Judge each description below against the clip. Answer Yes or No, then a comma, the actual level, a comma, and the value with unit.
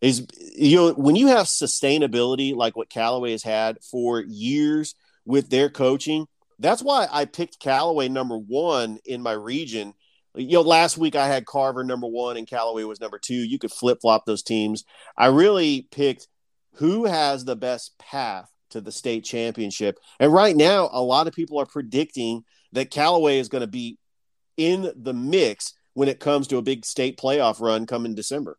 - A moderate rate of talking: Yes, average, 185 wpm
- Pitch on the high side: No, low, 135 Hz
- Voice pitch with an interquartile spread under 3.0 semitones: No, wide, 5.6 semitones